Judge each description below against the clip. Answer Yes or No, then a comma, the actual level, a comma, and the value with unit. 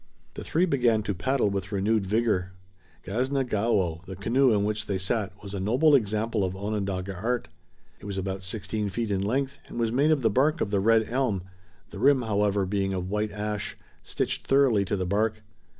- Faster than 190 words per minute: Yes, average, 200 wpm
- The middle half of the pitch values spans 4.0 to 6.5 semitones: No, average, 3.3 semitones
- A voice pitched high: No, low, 105 Hz